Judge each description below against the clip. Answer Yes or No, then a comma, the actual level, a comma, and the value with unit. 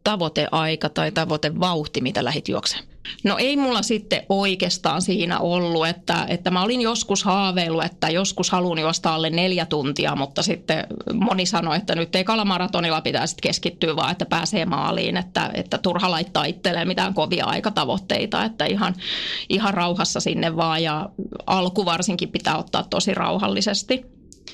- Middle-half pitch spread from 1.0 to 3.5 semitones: Yes, average, 3.2 semitones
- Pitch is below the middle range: No, medium, 180 Hz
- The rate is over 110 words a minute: Yes, average, 150 wpm